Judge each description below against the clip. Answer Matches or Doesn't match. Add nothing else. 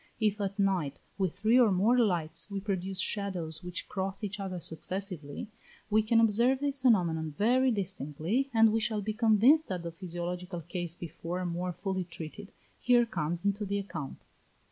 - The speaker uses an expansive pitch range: Doesn't match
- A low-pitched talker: Doesn't match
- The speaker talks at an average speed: Matches